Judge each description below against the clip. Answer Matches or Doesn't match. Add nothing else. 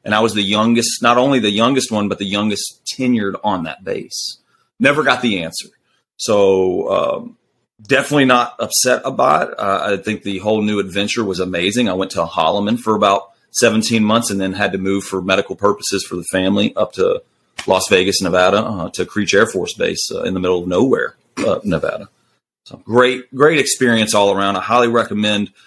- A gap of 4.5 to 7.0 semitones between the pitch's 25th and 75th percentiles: Doesn't match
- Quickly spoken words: Doesn't match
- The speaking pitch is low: Matches